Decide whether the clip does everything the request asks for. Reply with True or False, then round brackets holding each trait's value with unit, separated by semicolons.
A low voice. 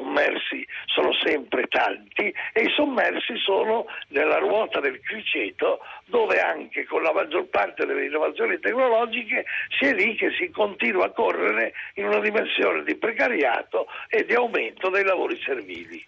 False (370 Hz)